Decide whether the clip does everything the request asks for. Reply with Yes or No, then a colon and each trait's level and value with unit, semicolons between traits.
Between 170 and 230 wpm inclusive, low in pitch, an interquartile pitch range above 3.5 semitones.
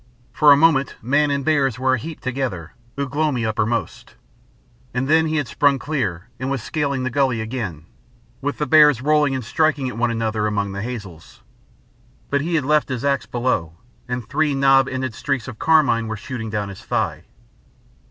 Yes: average, 185 wpm; low, 130 Hz; average, 4.2 semitones